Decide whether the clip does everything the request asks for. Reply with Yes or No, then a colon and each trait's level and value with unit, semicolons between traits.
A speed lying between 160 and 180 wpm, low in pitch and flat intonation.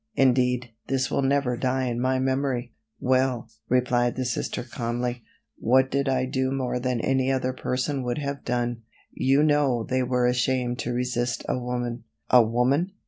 Yes: average, 165 wpm; low, 125 Hz; narrow, 1.4 semitones